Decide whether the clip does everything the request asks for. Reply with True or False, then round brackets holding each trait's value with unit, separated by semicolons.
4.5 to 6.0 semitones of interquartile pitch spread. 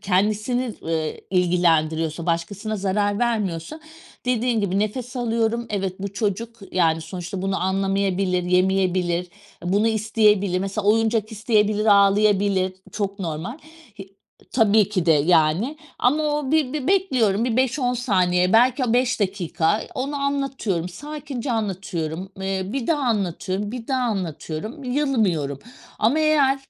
True (4.8 semitones)